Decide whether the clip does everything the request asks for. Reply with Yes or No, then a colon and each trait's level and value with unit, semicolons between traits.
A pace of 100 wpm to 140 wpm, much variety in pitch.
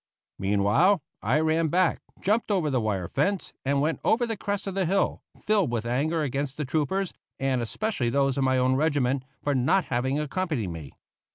No: average, 185 wpm; wide, 6.3 semitones